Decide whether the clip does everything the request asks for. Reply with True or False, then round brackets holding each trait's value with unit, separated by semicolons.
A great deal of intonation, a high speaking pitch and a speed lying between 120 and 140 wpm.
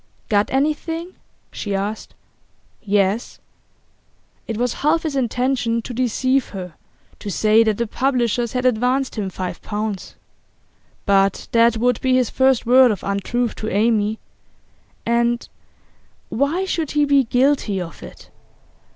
False (3.8 semitones; 235 Hz; 135 wpm)